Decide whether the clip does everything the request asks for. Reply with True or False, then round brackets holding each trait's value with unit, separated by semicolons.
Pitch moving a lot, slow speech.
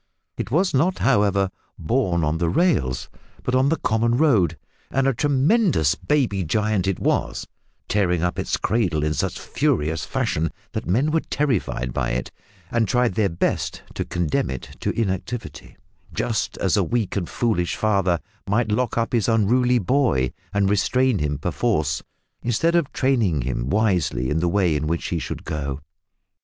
False (7.3 semitones; 165 wpm)